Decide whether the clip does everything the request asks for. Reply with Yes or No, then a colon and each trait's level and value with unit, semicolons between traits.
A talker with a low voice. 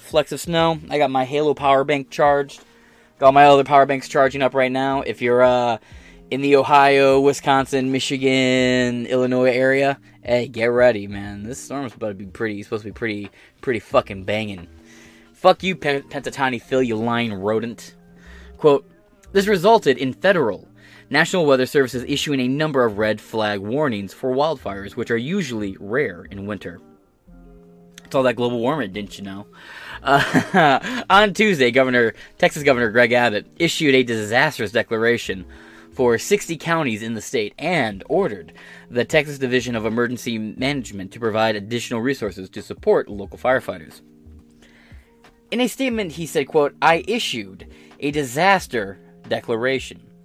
Yes: low, 125 Hz